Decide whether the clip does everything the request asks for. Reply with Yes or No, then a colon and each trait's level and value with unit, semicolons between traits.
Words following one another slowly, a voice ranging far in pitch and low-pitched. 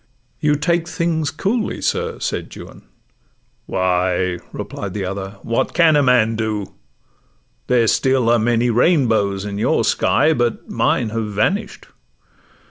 Yes: slow, 130 wpm; wide, 6.6 semitones; low, 115 Hz